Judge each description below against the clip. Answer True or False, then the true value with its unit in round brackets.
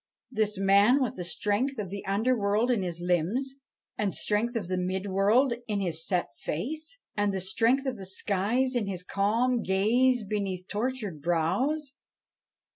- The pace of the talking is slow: False (165 wpm)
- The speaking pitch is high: True (205 Hz)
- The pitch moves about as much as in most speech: True (4.7 semitones)